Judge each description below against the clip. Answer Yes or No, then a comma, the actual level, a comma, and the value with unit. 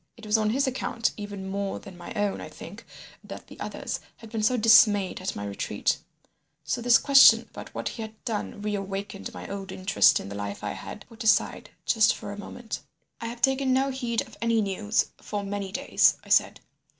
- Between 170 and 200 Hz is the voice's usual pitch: No, high, 210 Hz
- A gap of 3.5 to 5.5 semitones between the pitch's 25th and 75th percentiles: No, average, 2.8 semitones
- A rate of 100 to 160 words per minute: No, fast, 205 wpm